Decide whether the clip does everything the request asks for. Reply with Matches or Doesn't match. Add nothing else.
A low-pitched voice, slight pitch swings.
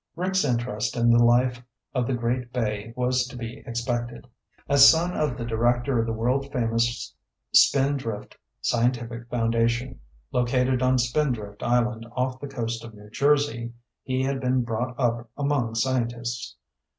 Matches